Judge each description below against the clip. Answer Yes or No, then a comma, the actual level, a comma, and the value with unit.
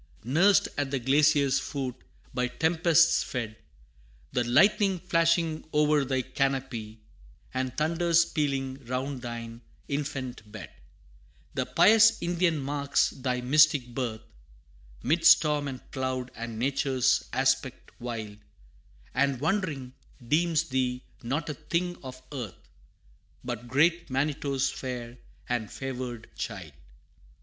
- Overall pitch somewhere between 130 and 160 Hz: Yes, low, 135 Hz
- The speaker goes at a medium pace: No, slow, 115 wpm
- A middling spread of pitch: Yes, average, 3.7 semitones